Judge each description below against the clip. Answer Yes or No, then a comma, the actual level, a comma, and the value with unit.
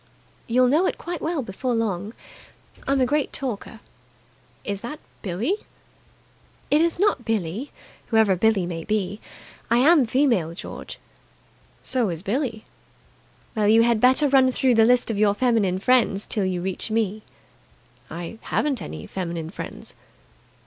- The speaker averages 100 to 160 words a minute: Yes, average, 145 wpm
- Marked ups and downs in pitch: No, average, 4.7 semitones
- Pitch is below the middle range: No, high, 225 Hz